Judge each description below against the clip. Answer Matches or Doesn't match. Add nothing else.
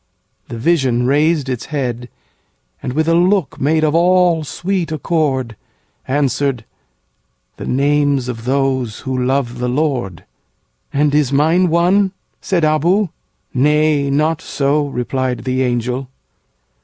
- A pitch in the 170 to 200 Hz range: Doesn't match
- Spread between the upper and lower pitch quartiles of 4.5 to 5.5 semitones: Doesn't match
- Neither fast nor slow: Doesn't match